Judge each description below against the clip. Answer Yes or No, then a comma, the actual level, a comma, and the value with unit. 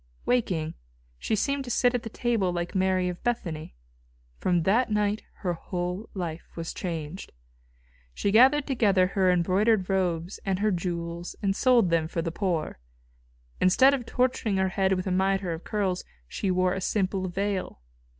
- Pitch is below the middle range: No, high, 190 Hz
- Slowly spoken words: No, average, 165 wpm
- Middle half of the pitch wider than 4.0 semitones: No, average, 3.2 semitones